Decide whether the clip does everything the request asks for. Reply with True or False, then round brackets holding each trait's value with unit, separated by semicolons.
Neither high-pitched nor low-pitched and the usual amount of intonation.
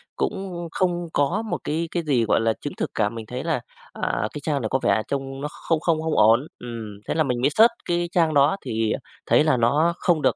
False (145 Hz; 6.0 semitones)